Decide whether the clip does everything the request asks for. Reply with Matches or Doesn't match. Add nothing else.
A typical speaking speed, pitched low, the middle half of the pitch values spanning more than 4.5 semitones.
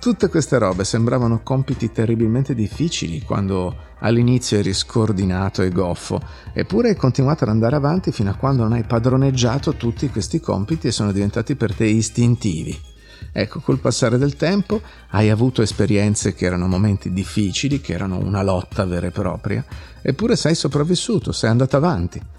Matches